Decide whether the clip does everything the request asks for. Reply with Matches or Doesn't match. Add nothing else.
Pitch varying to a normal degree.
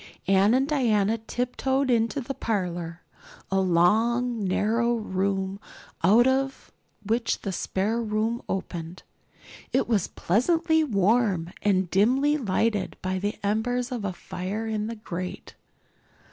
Matches